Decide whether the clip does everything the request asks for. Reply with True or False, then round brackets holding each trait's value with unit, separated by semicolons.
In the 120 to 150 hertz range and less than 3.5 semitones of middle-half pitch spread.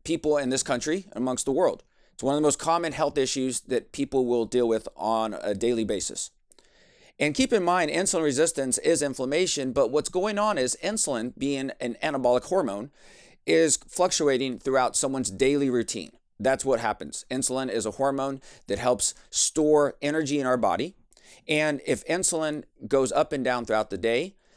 False (135 Hz; 4.0 semitones)